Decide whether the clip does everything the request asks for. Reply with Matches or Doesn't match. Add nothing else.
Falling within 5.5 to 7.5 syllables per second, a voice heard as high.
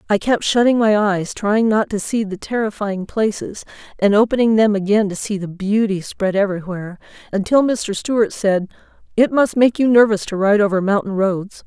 Doesn't match